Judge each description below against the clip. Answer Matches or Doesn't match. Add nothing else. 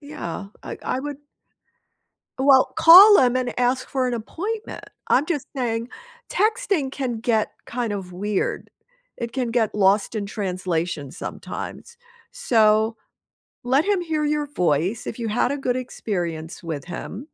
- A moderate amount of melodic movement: Doesn't match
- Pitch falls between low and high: Doesn't match